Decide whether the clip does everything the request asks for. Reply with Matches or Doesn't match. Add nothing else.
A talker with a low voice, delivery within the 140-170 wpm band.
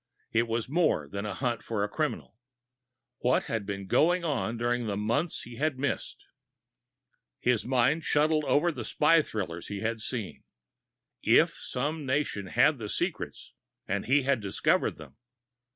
Matches